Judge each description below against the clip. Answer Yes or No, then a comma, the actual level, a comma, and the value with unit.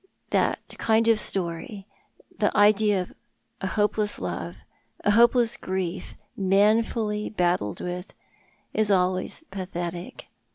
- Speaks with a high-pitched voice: Yes, high, 195 Hz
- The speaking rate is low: Yes, slow, 115 wpm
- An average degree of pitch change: Yes, average, 3.0 semitones